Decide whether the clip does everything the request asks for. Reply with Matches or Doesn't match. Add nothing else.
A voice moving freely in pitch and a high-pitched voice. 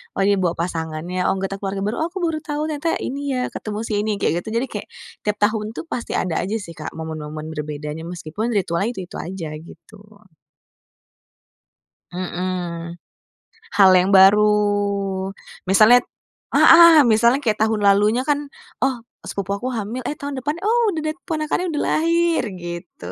Matches